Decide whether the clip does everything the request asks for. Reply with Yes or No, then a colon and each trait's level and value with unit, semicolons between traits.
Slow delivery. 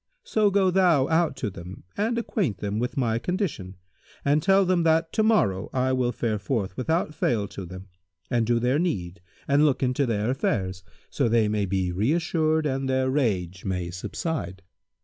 No: average, 180 wpm